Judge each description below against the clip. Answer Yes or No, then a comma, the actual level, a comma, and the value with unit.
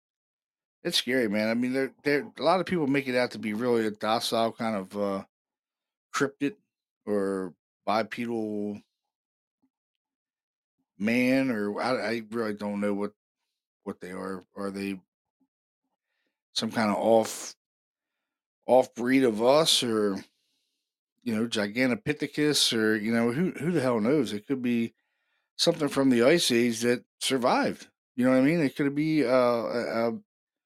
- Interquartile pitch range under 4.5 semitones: No, average, 4.8 semitones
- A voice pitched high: No, low, 120 Hz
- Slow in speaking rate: No, average, 155 wpm